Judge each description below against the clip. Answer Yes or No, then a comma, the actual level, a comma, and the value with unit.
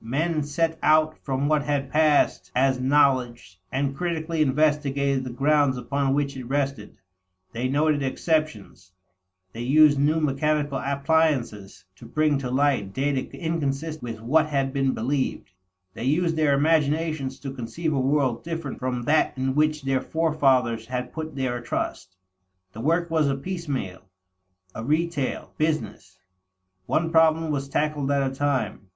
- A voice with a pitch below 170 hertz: Yes, medium, 140 Hz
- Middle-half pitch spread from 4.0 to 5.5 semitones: No, average, 3.0 semitones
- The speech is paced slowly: No, average, 145 wpm